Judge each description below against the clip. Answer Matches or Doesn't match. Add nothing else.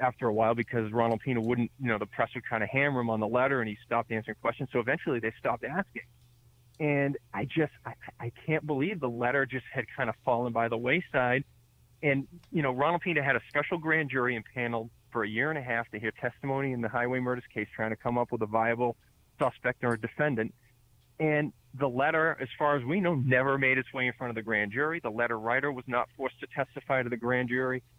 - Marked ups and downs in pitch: Doesn't match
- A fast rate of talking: Matches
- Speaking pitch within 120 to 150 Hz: Matches